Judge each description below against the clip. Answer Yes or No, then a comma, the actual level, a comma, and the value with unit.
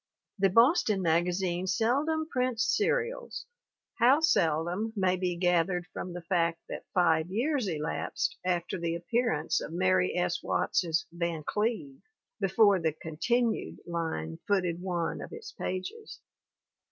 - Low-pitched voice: No, medium, 185 Hz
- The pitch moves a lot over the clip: Yes, wide, 5.9 semitones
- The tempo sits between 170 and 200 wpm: No, slow, 135 wpm